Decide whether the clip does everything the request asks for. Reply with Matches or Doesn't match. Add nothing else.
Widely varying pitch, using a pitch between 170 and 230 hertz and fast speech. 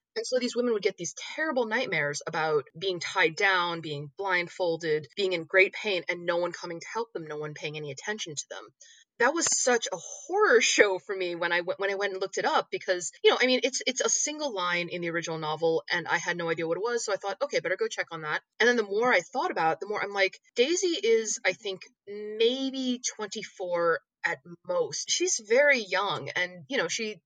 Matches